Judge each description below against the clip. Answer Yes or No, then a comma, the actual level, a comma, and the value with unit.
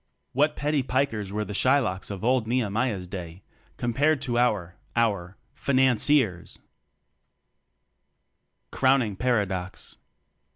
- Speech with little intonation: No, average, 4.9 semitones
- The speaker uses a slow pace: Yes, slow, 100 wpm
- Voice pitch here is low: Yes, low, 115 Hz